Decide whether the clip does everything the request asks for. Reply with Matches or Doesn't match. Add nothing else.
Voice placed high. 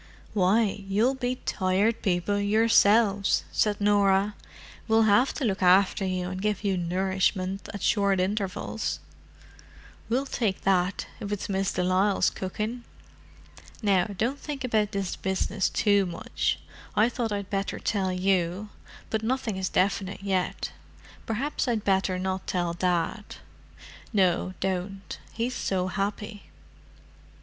Matches